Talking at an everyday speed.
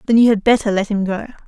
No: fast, 285 wpm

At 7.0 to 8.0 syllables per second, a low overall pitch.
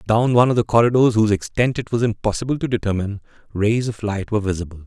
Yes: 7.1 syllables/s; low, 110 Hz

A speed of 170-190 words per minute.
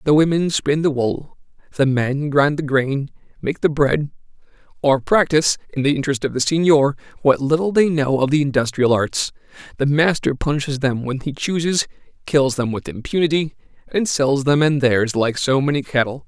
Yes: average, 180 wpm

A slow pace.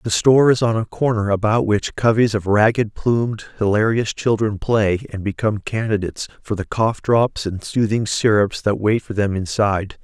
No: average, 180 wpm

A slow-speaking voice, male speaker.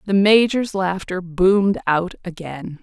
No: slow, 130 wpm; female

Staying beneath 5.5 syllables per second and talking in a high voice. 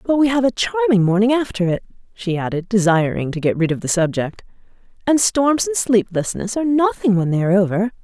No: 5.8 syllables/s; high, 210 Hz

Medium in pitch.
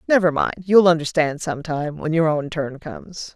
Yes: medium, 160 Hz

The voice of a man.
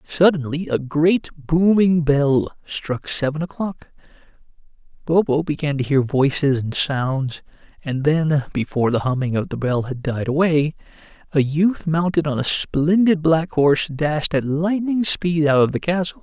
Yes: male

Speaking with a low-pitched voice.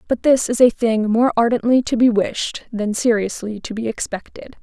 No: high, 230 Hz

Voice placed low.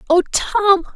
No: very high, 375 Hz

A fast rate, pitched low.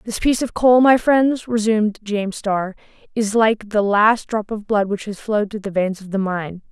No: fast, 225 wpm; high, 210 Hz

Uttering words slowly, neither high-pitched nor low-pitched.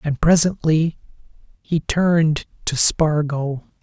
Yes: slow, 95 wpm; medium, 155 Hz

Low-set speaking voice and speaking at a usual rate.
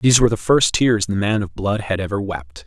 No: low, 105 Hz; fast, 270 wpm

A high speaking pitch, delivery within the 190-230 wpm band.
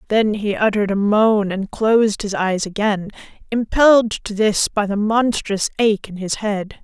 No: high, 210 Hz; average, 175 wpm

